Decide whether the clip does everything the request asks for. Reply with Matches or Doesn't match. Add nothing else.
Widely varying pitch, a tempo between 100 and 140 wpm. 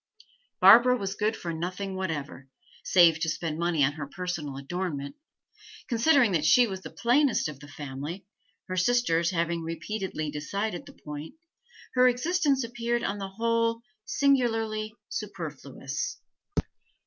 Matches